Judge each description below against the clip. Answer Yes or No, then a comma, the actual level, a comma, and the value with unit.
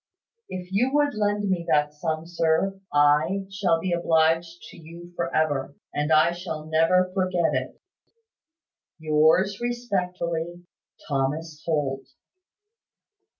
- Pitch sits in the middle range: Yes, medium, 170 Hz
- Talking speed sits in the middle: No, slow, 115 wpm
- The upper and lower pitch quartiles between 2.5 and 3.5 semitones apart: Yes, average, 2.8 semitones